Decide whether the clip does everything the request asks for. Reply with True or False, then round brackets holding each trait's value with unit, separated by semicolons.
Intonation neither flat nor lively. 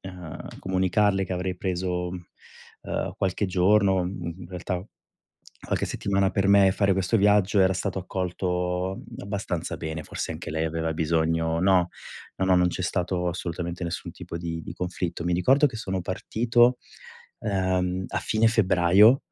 False (1.9 semitones)